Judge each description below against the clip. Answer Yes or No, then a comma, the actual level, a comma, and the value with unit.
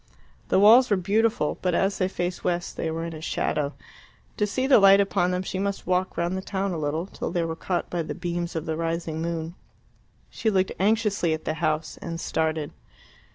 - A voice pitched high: No, medium, 175 Hz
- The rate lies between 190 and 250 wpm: Yes, fast, 205 wpm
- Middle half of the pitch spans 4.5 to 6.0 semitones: No, average, 3.1 semitones